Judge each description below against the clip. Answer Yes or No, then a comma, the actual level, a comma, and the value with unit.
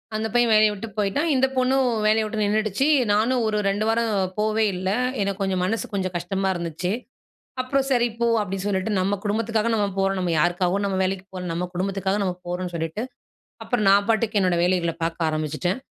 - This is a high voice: Yes, high, 200 Hz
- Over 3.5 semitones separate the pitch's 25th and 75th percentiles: No, average, 3.2 semitones